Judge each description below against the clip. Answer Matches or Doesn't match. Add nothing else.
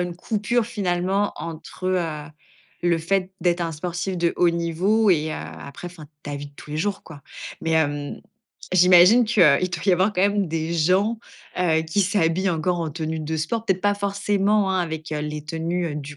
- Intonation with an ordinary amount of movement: Matches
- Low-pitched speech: Doesn't match